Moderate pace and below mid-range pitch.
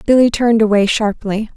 No: average, 155 wpm; high, 220 Hz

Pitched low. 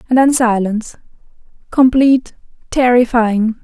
No: high, 240 Hz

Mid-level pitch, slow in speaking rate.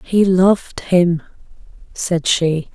Yes: medium, 175 Hz; slow, 110 wpm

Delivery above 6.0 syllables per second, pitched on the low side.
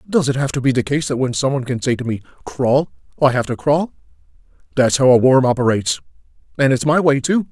Yes: 6.3 syllables/s; low, 130 Hz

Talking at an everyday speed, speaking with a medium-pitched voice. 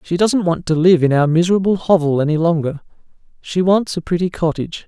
Yes: average, 195 wpm; medium, 170 Hz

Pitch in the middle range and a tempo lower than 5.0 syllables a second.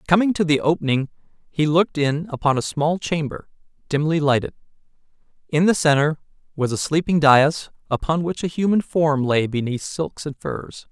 No: medium, 155 Hz; 5.1 syllables/s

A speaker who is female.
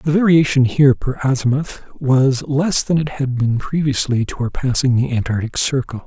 No: male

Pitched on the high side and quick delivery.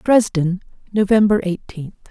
No: high, 195 Hz; slow, 85 wpm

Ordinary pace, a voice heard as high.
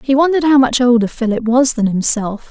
No: fast, 215 wpm; high, 245 Hz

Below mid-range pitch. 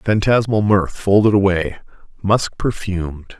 Yes: low, 100 Hz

